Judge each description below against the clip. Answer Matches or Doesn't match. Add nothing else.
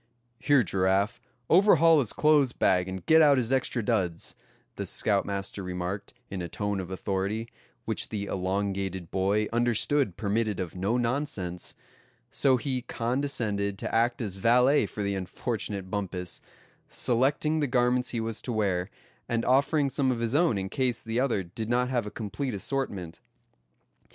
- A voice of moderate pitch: Doesn't match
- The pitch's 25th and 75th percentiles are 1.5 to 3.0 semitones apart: Doesn't match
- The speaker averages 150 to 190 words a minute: Matches